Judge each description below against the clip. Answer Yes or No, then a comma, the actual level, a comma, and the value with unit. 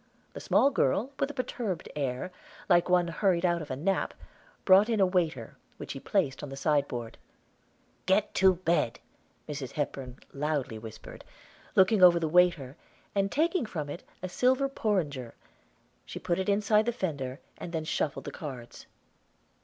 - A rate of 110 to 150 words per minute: No, average, 160 wpm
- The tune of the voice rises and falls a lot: Yes, wide, 5.7 semitones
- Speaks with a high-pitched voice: No, medium, 175 Hz